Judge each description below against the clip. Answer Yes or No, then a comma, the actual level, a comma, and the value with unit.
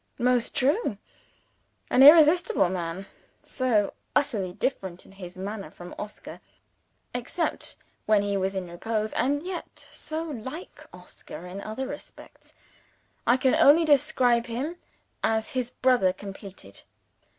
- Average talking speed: No, slow, 125 wpm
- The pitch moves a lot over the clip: Yes, wide, 6.0 semitones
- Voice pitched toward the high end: Yes, high, 230 Hz